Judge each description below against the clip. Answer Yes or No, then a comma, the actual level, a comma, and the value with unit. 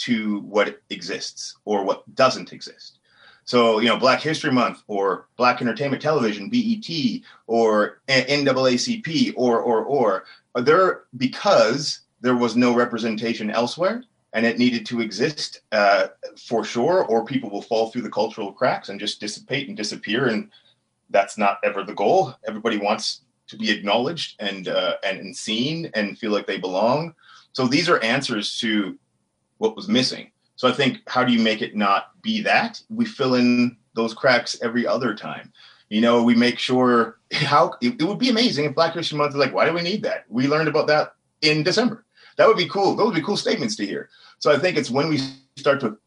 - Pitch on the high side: No, low, 130 Hz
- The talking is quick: No, average, 190 wpm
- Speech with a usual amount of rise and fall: No, wide, 6.1 semitones